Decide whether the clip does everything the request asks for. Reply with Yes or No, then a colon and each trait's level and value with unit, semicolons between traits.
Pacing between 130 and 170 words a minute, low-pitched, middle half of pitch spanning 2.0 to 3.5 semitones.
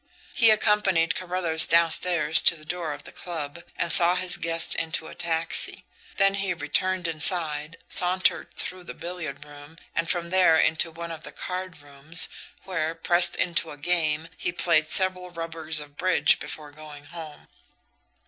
No: average, 160 wpm; medium, 165 Hz; narrow, 2.6 semitones